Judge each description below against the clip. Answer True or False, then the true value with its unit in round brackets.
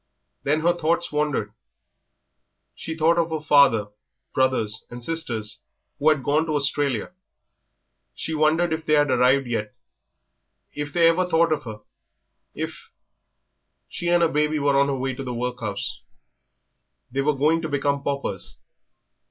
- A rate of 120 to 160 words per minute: True (150 wpm)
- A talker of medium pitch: True (145 Hz)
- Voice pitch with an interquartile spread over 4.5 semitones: False (3.5 semitones)